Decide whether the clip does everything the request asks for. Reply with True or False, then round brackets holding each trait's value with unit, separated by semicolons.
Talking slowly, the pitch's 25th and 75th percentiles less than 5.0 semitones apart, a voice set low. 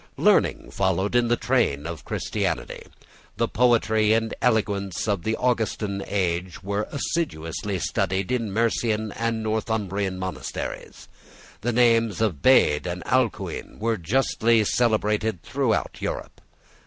True (120 wpm; 3.5 semitones; 110 Hz)